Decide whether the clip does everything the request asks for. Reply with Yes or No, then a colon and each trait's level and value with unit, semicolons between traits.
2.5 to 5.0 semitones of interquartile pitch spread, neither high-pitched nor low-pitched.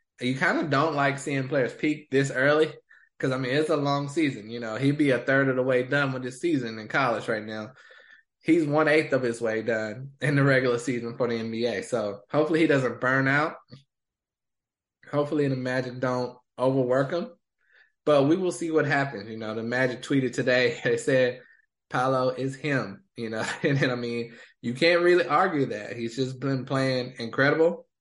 No: average, 3.2 semitones; low, 130 Hz